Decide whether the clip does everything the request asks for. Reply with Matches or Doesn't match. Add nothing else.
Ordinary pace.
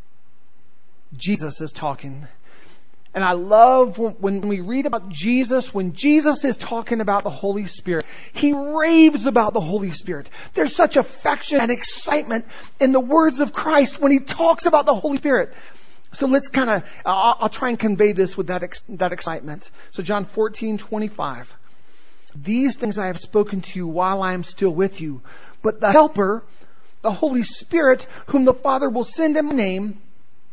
Matches